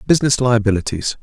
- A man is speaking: Yes, male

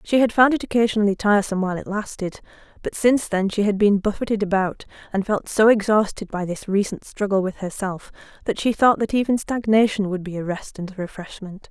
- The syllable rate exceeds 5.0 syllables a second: Yes, 5.9 syllables/s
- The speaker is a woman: Yes, female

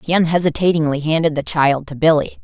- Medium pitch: Yes, medium, 155 Hz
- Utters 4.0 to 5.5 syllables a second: No, 6.0 syllables/s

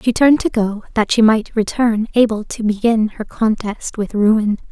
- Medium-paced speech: Yes, average, 190 wpm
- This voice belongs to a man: No, female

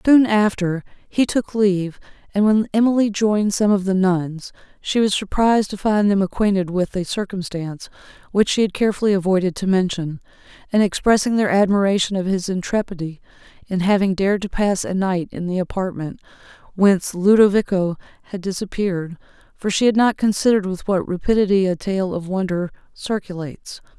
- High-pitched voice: Yes, high, 195 Hz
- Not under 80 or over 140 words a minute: No, average, 160 wpm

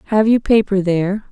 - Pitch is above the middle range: Yes, high, 200 Hz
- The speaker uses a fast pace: No, average, 185 wpm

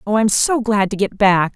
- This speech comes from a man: No, female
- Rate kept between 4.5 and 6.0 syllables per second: Yes, 5.6 syllables/s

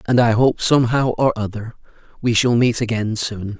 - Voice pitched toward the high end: No, low, 115 Hz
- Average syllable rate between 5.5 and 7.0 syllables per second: No, 5.2 syllables/s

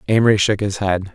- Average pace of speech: No, fast, 210 wpm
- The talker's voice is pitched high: No, low, 100 Hz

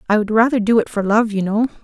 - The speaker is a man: No, female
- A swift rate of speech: Yes, fast, 295 wpm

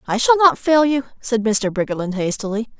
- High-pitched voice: Yes, high, 240 Hz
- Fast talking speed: No, average, 195 wpm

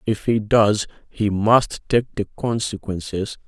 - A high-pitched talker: No, low, 105 Hz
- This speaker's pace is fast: No, average, 140 wpm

